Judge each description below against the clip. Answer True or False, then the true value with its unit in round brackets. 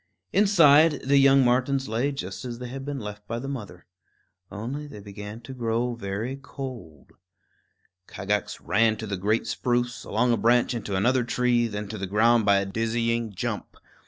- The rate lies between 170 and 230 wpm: True (175 wpm)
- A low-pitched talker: True (115 Hz)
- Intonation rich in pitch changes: False (3.8 semitones)